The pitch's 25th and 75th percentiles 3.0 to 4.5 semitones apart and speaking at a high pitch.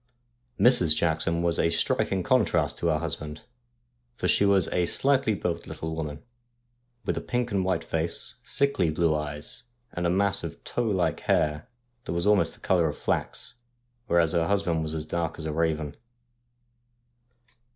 No: average, 3.5 semitones; very low, 85 Hz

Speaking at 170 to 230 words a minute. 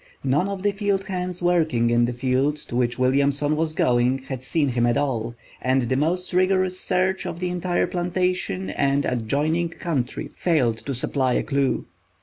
Yes: average, 175 wpm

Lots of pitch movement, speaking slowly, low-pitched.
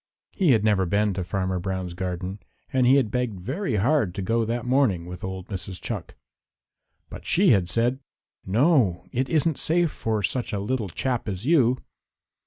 No: wide, 5.7 semitones; average, 180 wpm; low, 110 Hz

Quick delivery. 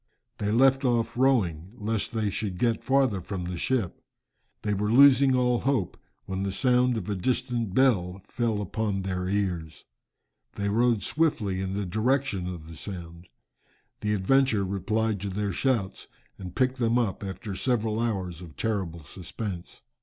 No: average, 160 wpm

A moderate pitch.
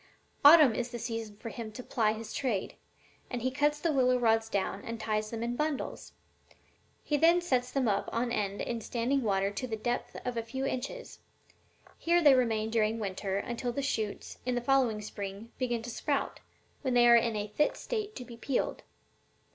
No: high, 235 Hz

